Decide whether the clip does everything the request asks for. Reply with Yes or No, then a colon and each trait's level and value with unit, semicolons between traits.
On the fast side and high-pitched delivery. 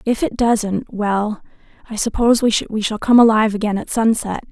No: average, 175 wpm; high, 220 Hz